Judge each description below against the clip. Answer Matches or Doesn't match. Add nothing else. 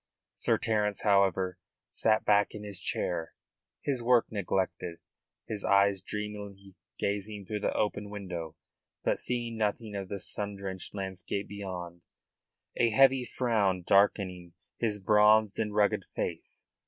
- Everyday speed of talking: Doesn't match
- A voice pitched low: Matches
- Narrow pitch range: Matches